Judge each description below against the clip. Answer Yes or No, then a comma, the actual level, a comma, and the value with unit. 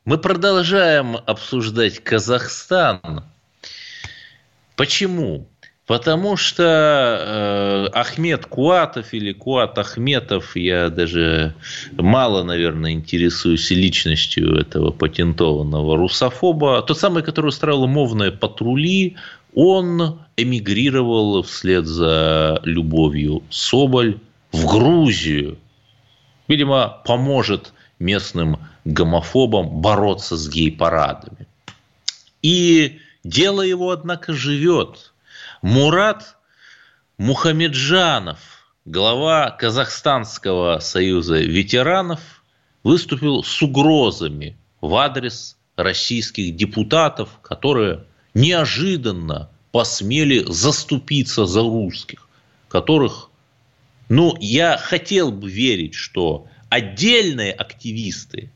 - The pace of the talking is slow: Yes, slow, 80 wpm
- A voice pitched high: No, low, 120 Hz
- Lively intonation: Yes, wide, 8.5 semitones